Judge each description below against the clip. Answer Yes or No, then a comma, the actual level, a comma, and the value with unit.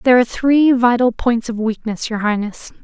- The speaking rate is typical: Yes, average, 190 wpm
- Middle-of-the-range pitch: No, high, 235 Hz